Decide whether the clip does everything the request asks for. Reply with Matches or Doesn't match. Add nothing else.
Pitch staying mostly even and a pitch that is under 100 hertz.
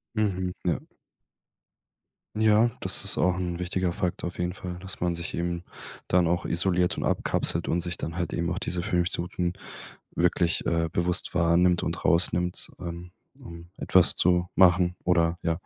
Matches